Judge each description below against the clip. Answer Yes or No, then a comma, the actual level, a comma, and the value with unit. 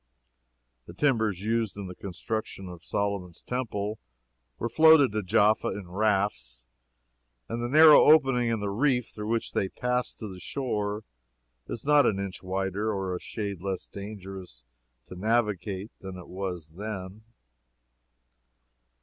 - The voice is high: No, low, 105 Hz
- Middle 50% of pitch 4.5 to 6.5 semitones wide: No, average, 3.4 semitones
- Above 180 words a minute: No, average, 140 wpm